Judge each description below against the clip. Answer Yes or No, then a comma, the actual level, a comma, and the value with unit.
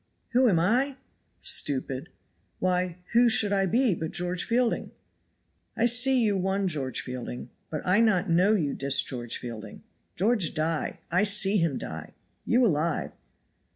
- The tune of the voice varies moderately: No, wide, 6.3 semitones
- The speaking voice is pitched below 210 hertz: Yes, medium, 185 Hz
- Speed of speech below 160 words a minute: Yes, average, 150 wpm